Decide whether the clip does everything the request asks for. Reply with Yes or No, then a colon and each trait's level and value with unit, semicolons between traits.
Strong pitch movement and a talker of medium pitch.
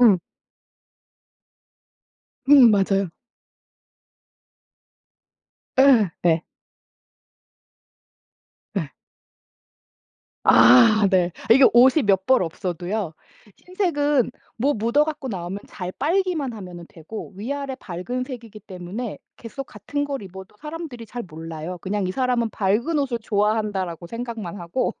No: wide, 6.2 semitones; high, 215 Hz